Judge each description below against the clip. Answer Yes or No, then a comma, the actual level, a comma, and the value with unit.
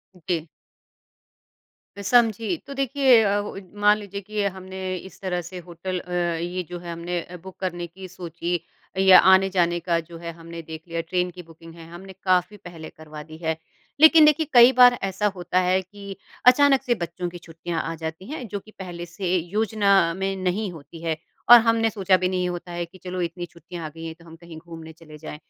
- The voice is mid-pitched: Yes, medium, 180 Hz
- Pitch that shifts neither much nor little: Yes, average, 3.0 semitones